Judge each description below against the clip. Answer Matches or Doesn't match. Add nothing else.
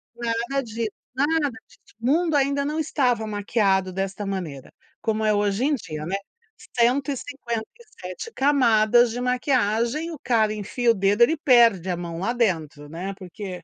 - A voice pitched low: Doesn't match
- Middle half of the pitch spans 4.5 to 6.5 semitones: Matches